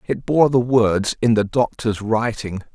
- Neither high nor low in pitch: No, low, 115 Hz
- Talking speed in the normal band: Yes, average, 175 wpm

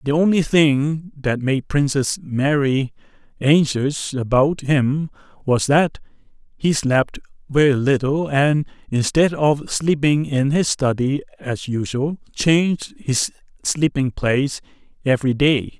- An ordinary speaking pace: No, slow, 120 wpm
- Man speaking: Yes, male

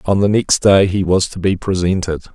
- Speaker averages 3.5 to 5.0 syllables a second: No, 5.2 syllables/s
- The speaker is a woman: No, male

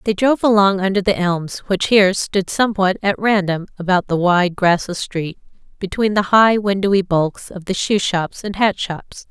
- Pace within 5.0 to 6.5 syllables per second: No, 4.8 syllables/s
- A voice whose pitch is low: No, high, 190 Hz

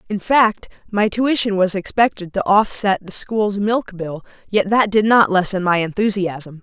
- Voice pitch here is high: Yes, high, 200 Hz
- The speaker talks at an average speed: Yes, average, 170 wpm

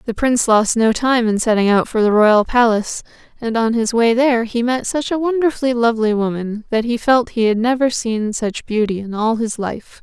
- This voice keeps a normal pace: No, fast, 220 wpm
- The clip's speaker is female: Yes, female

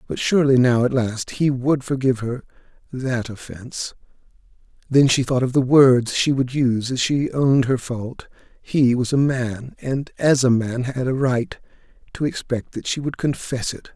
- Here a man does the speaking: Yes, male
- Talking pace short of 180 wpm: No, average, 185 wpm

